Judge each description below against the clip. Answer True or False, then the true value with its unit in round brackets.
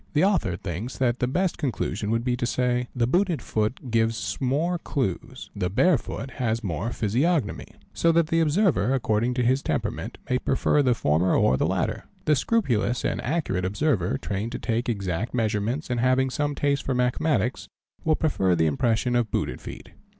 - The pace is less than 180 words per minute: False (185 wpm)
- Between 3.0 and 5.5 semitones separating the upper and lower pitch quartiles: True (5.0 semitones)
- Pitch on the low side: True (125 Hz)